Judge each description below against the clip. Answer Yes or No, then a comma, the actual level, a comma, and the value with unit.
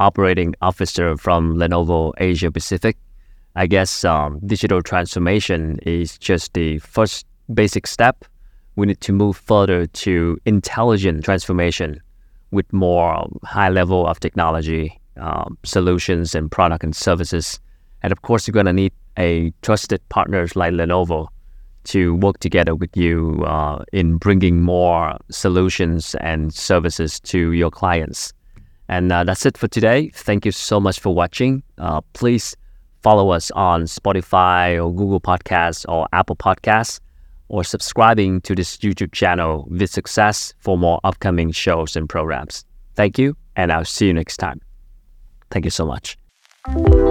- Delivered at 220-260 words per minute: No, slow, 145 wpm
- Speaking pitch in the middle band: No, very low, 90 Hz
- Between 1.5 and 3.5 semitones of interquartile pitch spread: Yes, average, 3.0 semitones